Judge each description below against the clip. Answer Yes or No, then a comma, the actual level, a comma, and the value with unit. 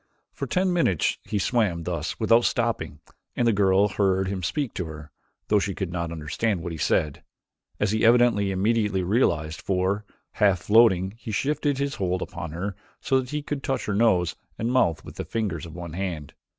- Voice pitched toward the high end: No, low, 100 Hz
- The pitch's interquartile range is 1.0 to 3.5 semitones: No, average, 5.0 semitones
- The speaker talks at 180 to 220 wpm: Yes, average, 190 wpm